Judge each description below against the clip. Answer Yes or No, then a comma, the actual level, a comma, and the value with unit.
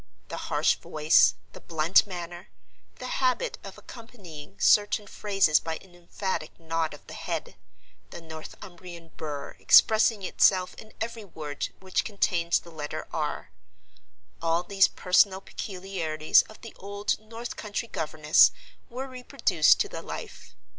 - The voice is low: No, medium, 175 Hz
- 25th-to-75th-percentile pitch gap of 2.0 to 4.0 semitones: No, average, 4.8 semitones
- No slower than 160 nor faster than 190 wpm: No, slow, 135 wpm